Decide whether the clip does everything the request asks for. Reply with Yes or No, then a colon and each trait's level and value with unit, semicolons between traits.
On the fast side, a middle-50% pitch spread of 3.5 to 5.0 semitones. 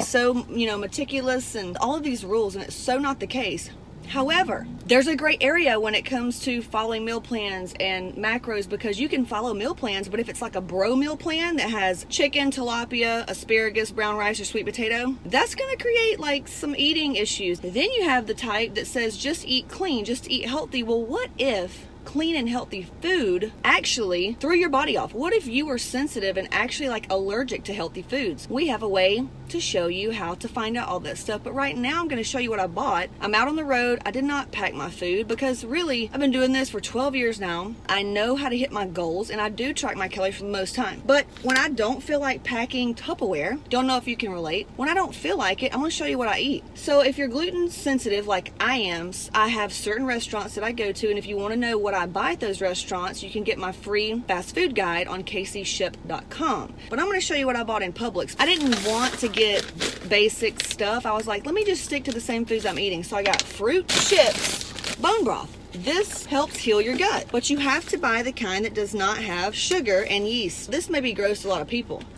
Yes: fast, 240 wpm; average, 4.7 semitones